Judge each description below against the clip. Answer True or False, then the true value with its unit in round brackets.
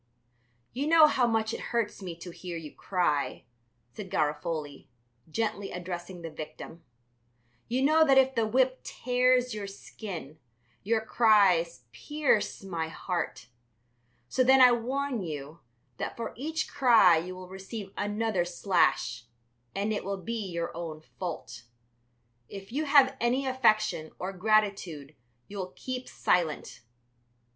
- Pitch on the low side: False (200 Hz)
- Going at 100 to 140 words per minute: True (135 wpm)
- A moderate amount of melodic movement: False (6.1 semitones)